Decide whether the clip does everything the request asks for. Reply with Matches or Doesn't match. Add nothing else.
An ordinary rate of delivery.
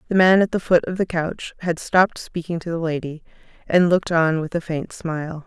Doesn't match